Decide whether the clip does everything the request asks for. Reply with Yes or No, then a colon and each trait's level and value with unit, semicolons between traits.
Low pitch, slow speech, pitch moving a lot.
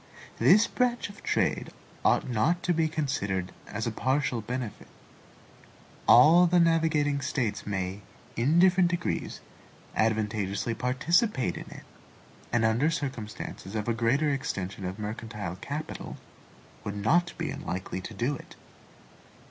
Yes: low, 125 Hz; slow, 130 wpm; wide, 7.3 semitones